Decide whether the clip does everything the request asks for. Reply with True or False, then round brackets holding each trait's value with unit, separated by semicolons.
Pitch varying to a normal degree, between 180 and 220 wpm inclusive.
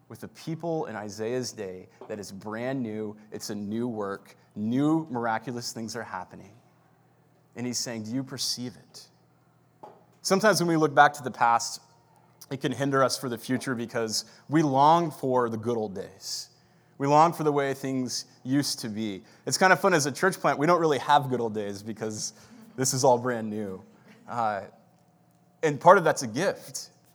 True (4.5 semitones; 190 wpm)